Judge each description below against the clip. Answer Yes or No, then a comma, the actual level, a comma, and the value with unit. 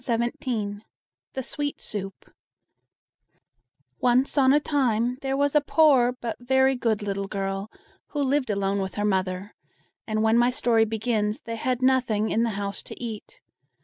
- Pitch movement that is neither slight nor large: Yes, average, 4.0 semitones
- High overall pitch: Yes, high, 230 Hz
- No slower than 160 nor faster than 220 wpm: No, average, 150 wpm